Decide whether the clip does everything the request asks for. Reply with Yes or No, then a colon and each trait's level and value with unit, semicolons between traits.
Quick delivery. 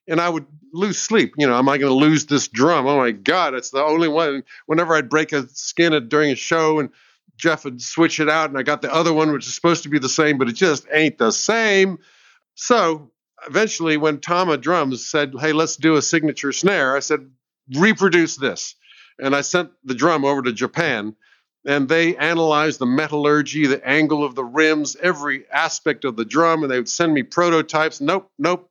Yes: fast, 210 wpm